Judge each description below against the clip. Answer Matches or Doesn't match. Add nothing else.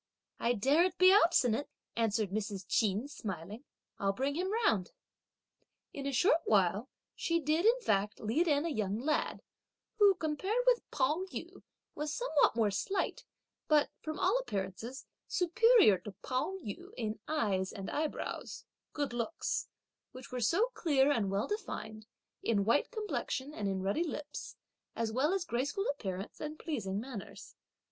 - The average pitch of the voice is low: Doesn't match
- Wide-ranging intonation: Matches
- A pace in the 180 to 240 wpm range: Doesn't match